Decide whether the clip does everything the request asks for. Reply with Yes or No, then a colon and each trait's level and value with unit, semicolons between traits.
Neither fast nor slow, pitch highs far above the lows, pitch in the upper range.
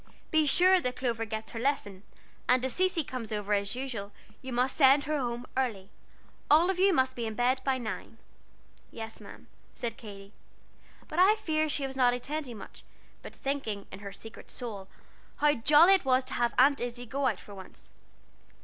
No: average, 185 wpm; average, 4.4 semitones; very high, 255 Hz